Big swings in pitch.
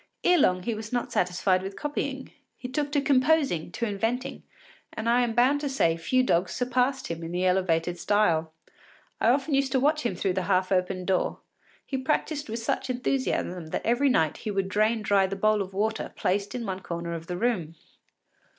Yes: wide, 5.8 semitones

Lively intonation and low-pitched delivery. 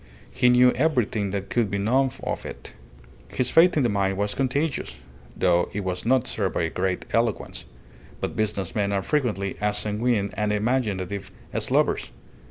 No: average, 4.1 semitones; low, 105 Hz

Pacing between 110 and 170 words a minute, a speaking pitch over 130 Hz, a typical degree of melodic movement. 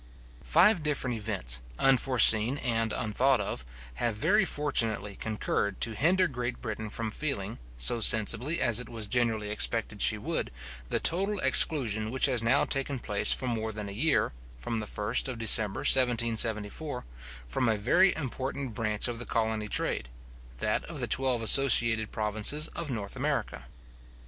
No: average, 155 wpm; low, 115 Hz; average, 3.8 semitones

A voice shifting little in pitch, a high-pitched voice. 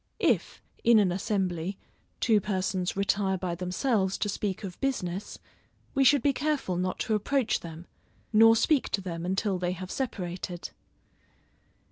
No: average, 3.7 semitones; high, 195 Hz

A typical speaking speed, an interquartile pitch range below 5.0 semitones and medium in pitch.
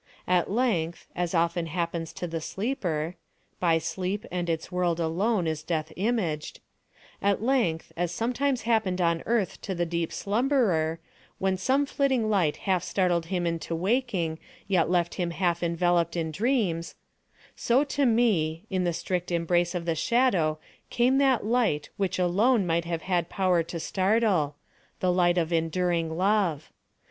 Yes: average, 150 wpm; average, 4.0 semitones; medium, 180 Hz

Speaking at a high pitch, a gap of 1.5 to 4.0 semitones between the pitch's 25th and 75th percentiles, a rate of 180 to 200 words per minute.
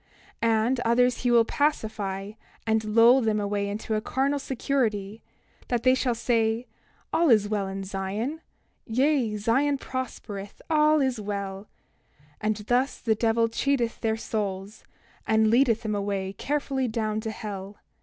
No: high, 225 Hz; average, 3.4 semitones; average, 140 wpm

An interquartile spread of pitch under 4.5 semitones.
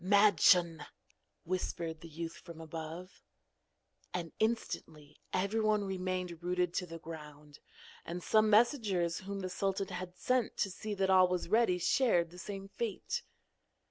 Yes: average, 3.2 semitones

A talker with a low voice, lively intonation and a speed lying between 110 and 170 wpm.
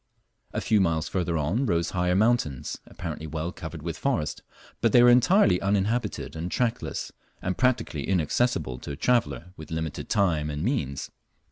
Yes: very low, 90 Hz; wide, 6.6 semitones; average, 160 wpm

